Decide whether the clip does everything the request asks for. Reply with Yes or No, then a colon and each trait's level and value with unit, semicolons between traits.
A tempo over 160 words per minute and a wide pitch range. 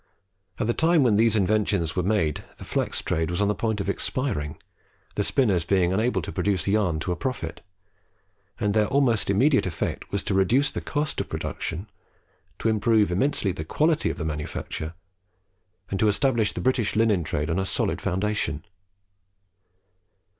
No: average, 170 wpm; average, 4.6 semitones